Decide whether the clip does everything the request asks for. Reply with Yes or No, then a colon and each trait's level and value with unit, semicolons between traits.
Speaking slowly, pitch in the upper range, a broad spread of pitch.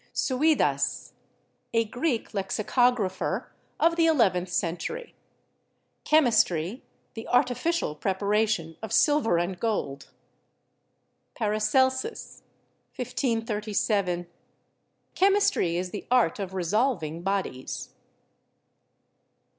Yes: slow, 85 wpm; high, 215 Hz; wide, 5.9 semitones